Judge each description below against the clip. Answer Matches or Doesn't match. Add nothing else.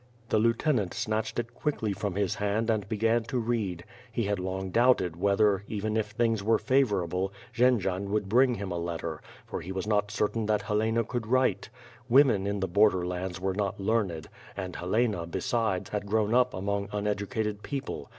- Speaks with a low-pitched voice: Matches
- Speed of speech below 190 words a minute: Matches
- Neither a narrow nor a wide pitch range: Matches